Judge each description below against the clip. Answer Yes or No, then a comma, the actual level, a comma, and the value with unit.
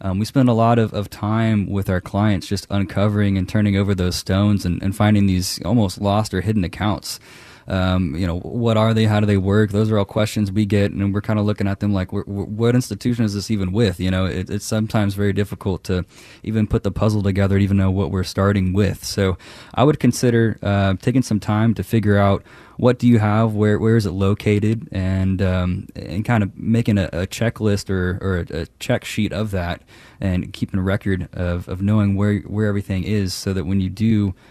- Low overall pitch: Yes, low, 100 Hz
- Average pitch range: No, narrow, 2.0 semitones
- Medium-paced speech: No, fast, 230 wpm